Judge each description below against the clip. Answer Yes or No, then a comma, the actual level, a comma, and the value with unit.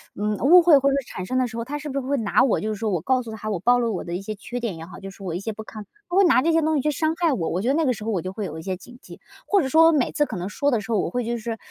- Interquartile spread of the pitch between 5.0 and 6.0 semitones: Yes, wide, 5.5 semitones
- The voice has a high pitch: Yes, high, 235 Hz